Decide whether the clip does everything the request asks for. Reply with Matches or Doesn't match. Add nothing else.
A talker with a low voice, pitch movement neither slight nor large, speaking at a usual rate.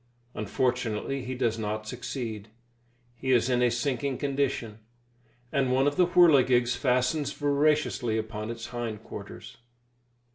Doesn't match